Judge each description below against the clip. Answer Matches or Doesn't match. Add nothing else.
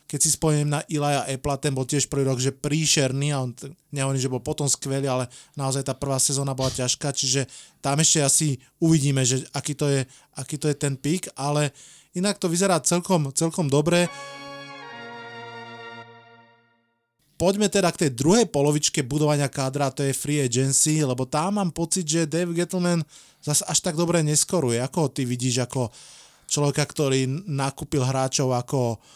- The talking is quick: Matches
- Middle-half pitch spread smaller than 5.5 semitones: Matches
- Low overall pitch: Doesn't match